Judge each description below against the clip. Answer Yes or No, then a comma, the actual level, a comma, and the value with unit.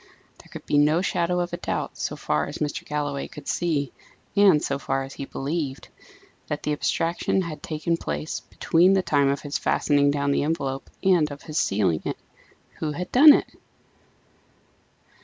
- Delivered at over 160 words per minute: Yes, average, 175 wpm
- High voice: No, medium, 150 Hz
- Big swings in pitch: No, average, 3.2 semitones